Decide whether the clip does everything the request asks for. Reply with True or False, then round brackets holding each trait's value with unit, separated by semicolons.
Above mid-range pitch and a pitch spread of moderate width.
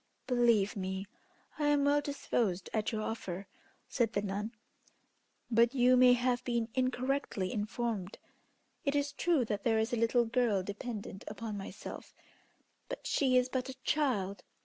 True (235 Hz; 3.7 semitones)